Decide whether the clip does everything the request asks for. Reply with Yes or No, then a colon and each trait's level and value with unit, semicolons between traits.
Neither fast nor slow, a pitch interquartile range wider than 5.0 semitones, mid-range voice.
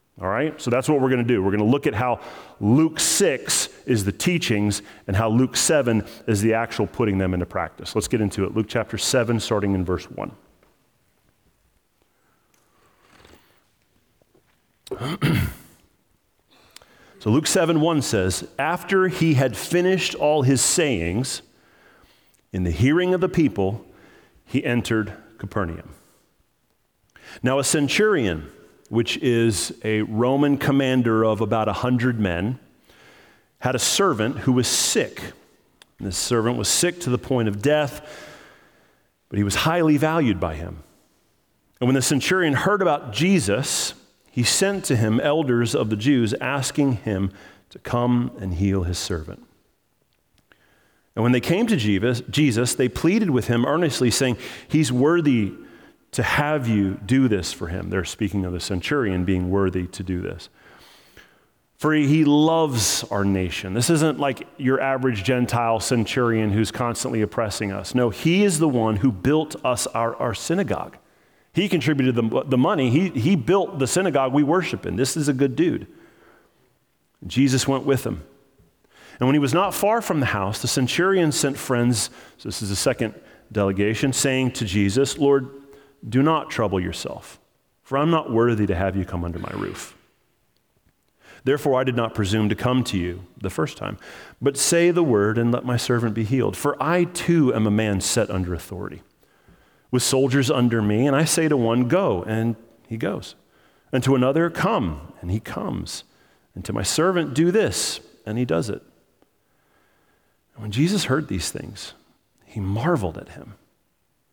No: average, 165 wpm; wide, 5.5 semitones; low, 120 Hz